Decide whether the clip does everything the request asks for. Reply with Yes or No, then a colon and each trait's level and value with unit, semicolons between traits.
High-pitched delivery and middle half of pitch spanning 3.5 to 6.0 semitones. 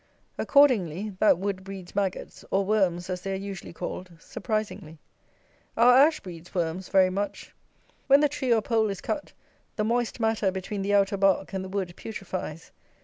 No: high, 195 Hz; average, 2.9 semitones